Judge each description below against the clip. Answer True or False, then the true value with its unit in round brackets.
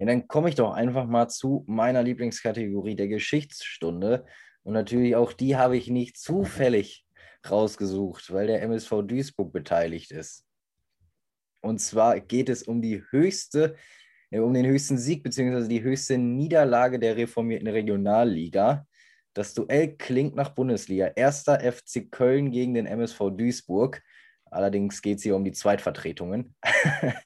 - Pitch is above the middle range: False (120 Hz)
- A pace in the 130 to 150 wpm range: True (140 wpm)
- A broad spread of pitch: False (3.5 semitones)